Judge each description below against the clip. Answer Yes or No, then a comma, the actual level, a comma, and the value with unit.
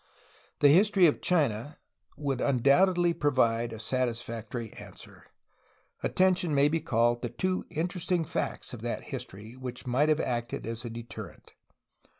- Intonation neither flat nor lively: No, wide, 5.7 semitones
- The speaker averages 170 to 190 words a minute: No, average, 145 wpm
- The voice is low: Yes, low, 130 Hz